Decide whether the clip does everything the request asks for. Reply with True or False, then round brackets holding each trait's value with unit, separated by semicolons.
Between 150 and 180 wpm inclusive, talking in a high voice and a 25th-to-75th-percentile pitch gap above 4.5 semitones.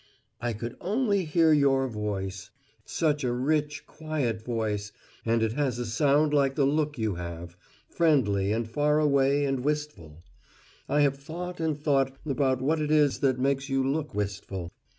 False (160 wpm; 135 Hz; 4.9 semitones)